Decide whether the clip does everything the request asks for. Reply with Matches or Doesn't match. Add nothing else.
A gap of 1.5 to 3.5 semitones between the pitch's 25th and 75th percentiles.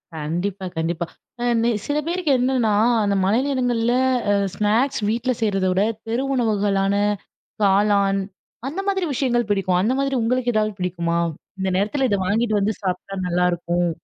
Doesn't match